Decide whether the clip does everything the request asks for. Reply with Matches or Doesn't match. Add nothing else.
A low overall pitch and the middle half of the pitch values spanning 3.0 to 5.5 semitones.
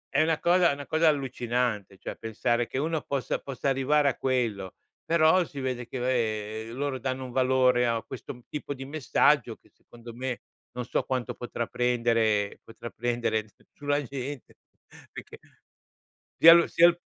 Matches